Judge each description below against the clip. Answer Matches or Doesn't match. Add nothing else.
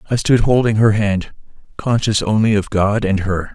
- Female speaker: Doesn't match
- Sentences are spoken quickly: Doesn't match